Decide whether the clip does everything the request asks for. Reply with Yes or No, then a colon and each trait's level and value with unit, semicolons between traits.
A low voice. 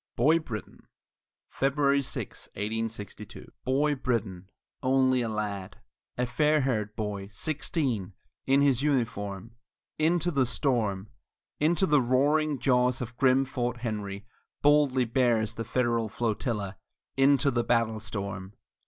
Yes: low, 120 Hz